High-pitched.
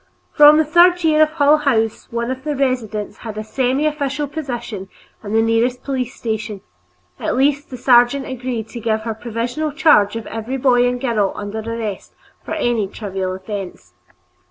Yes: high, 240 Hz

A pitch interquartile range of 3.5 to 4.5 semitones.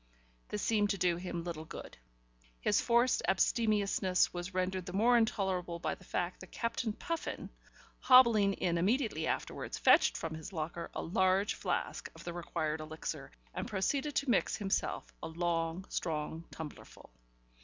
Yes: average, 4.0 semitones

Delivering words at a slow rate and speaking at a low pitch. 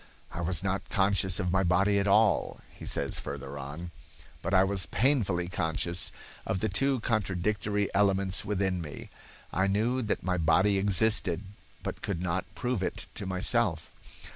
No: average, 160 wpm; very low, 95 Hz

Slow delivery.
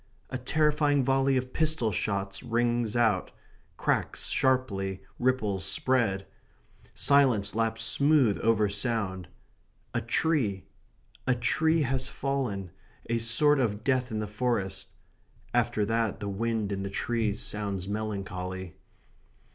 Yes: slow, 120 wpm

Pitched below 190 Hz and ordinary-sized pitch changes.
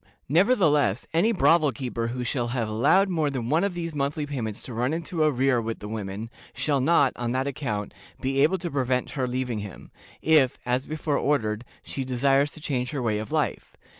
Yes: low, 135 Hz; average, 4.2 semitones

